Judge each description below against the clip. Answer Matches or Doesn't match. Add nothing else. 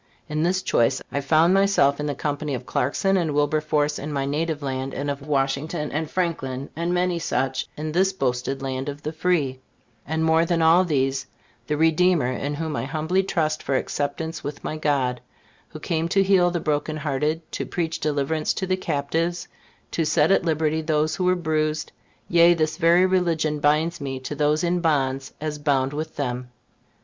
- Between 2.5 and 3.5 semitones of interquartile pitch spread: Matches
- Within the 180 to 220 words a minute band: Matches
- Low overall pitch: Doesn't match